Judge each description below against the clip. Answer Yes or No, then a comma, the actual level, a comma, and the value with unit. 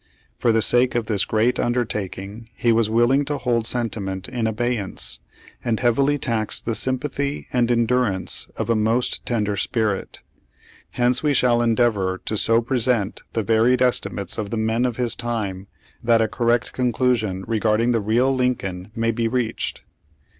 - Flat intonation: Yes, narrow, 2.2 semitones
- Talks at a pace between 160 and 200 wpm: Yes, average, 165 wpm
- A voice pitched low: Yes, low, 115 Hz